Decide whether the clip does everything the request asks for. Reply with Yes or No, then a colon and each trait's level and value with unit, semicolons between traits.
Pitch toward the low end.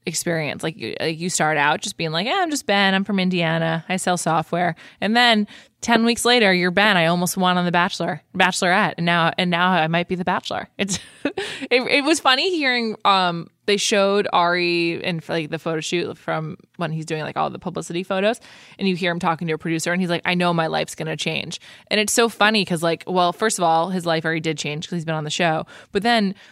No: medium, 180 Hz